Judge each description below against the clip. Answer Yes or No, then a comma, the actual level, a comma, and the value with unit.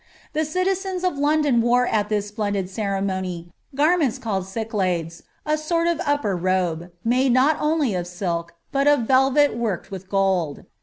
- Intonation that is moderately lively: No, wide, 7.5 semitones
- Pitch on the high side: Yes, high, 225 Hz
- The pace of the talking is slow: No, average, 155 wpm